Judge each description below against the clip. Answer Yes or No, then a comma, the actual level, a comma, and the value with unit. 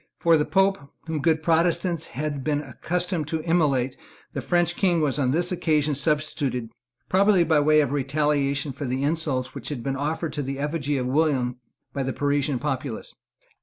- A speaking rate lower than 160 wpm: No, average, 175 wpm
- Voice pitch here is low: No, medium, 150 Hz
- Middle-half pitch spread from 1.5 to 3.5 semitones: Yes, average, 3.0 semitones